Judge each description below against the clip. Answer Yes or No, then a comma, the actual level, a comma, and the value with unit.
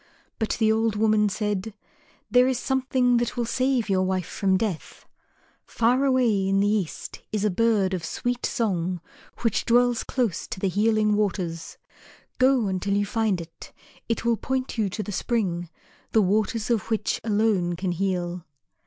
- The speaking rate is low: No, average, 165 wpm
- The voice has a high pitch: Yes, high, 215 Hz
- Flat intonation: No, average, 3.7 semitones